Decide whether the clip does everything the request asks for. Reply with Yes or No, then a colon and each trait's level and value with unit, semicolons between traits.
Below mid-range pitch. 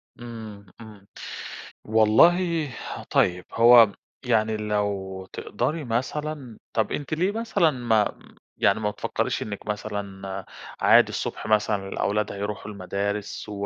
Yes: low, 105 Hz